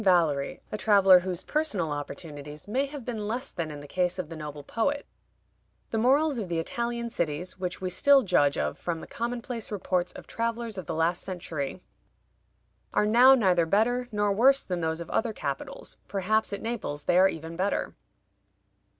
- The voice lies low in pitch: No, high, 190 Hz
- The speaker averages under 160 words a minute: No, average, 180 wpm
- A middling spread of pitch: No, wide, 5.9 semitones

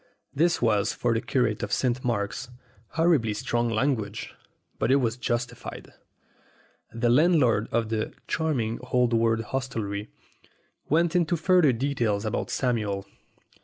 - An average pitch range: Yes, average, 3.6 semitones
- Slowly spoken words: Yes, slow, 130 wpm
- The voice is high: No, low, 120 Hz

